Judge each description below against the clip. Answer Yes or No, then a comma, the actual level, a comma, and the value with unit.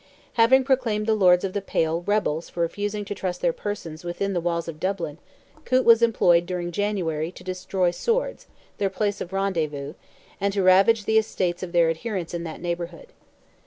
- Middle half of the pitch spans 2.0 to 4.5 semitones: Yes, average, 3.3 semitones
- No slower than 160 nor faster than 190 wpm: Yes, average, 185 wpm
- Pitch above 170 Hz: Yes, medium, 185 Hz